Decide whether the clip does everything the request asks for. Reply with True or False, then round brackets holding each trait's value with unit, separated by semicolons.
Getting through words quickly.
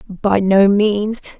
False (130 wpm)